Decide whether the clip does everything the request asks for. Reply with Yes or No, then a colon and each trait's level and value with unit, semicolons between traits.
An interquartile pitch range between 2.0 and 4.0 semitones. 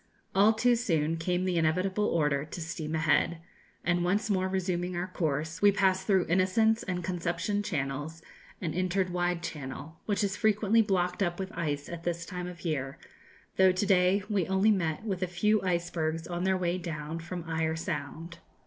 Yes: average, 2.7 semitones